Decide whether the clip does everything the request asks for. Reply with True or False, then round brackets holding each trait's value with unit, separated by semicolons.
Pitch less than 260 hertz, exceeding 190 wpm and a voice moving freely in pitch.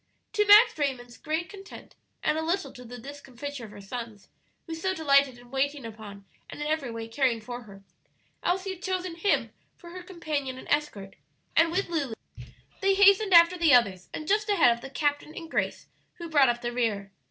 False (290 Hz; 200 wpm; 6.2 semitones)